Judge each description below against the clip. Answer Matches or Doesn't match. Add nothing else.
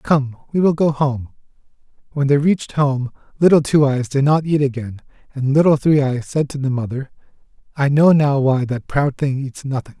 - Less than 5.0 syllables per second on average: Doesn't match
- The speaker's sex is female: Doesn't match